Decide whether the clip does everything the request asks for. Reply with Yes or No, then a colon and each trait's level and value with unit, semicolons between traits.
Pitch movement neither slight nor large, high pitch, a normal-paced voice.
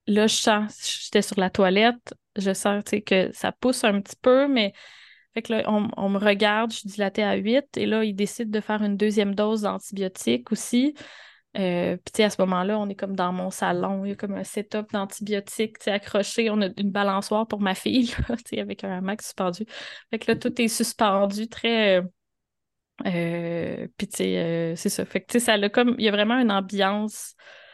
No: narrow, 2.3 semitones; high, 210 Hz; average, 200 wpm